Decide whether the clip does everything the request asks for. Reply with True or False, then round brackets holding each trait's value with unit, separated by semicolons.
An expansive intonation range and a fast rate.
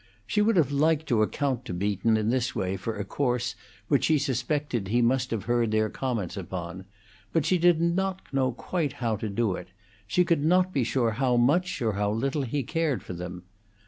True (5.9 semitones; 210 wpm)